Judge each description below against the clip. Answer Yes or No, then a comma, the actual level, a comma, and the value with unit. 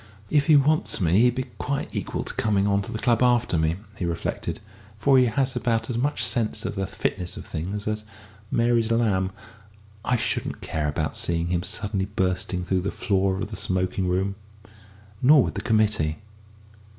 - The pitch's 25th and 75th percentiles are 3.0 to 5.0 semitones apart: Yes, average, 4.2 semitones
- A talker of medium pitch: No, low, 105 Hz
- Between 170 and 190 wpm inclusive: Yes, average, 185 wpm